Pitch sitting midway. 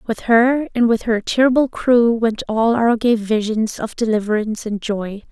No: high, 230 Hz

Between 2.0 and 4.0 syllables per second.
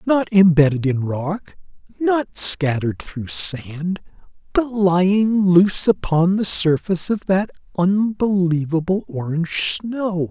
Yes: 3.8 syllables/s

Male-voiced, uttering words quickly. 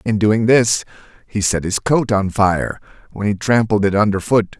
No: male; average, 195 wpm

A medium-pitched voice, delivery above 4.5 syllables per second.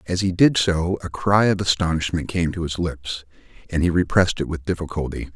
No: very low, 85 Hz; 5.5 syllables/s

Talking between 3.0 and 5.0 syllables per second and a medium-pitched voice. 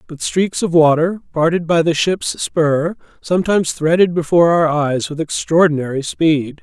Yes: 4.8 syllables/s; medium, 160 Hz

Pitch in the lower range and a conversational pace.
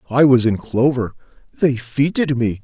Yes: low, 130 Hz; average, 160 wpm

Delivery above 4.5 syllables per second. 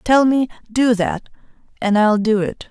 No: 4.2 syllables/s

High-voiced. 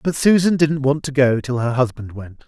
No: low, 135 Hz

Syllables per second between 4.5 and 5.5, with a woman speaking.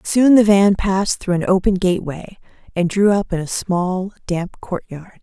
Yes: 4.6 syllables/s; female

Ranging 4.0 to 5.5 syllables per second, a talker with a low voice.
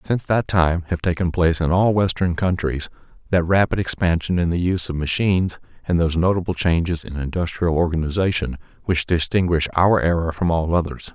No: 5.7 syllables/s; very low, 85 Hz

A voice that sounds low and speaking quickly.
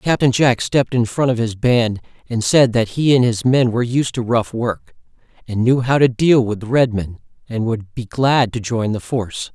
Yes: low, 120 Hz; fast, 240 wpm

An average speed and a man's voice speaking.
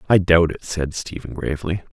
Yes: average, 185 wpm; male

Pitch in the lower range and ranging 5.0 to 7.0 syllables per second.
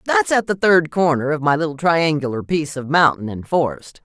No: medium, 155 Hz; 5.4 syllables/s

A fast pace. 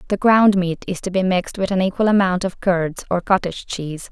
Yes: fast, 235 wpm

